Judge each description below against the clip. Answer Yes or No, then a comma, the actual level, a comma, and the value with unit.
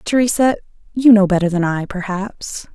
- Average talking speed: Yes, average, 155 wpm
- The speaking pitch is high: Yes, high, 205 Hz